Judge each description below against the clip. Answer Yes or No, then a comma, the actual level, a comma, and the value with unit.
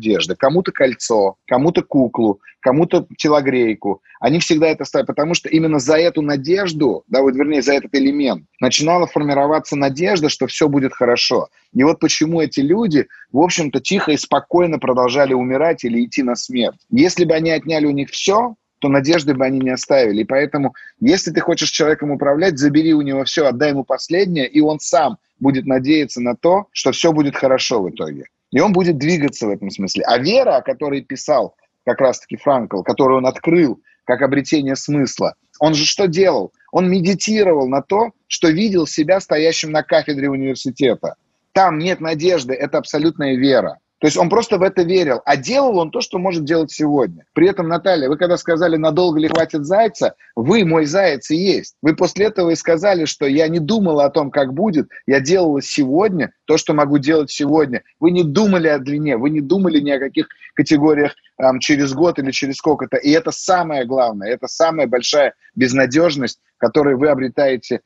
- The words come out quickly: Yes, fast, 185 wpm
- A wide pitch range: No, average, 3.9 semitones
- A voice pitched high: No, medium, 155 Hz